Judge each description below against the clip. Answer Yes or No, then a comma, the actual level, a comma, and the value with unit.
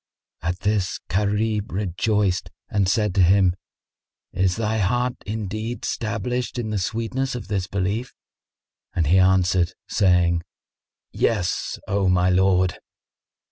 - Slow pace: Yes, slow, 120 wpm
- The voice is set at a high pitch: No, low, 100 Hz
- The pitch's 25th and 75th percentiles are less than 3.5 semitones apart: Yes, average, 3.1 semitones